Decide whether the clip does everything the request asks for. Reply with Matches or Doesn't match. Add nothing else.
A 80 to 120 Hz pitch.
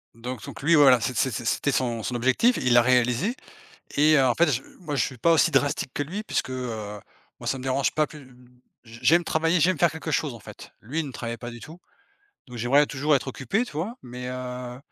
Doesn't match